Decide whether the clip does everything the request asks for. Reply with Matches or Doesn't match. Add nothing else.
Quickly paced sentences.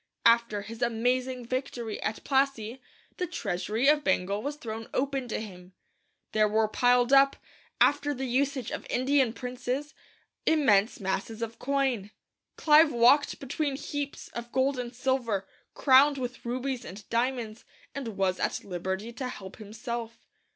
Doesn't match